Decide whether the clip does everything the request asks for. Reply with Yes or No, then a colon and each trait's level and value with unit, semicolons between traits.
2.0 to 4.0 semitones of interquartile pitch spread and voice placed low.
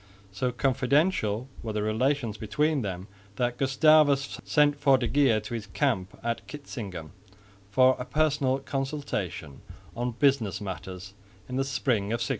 No: average, 4.8 semitones; low, 125 Hz